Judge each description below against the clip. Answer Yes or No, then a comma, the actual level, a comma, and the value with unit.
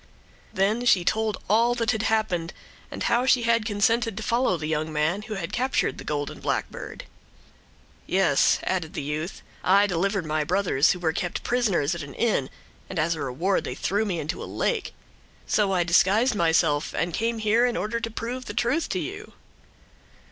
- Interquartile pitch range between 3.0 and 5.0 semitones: No, wide, 5.6 semitones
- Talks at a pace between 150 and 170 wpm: No, average, 185 wpm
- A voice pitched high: Yes, high, 195 Hz